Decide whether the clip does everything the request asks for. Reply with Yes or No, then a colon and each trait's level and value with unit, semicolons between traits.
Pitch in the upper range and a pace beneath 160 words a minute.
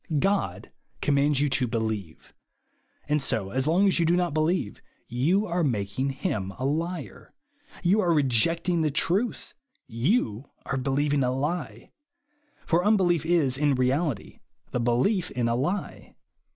No: medium, 145 Hz; average, 140 wpm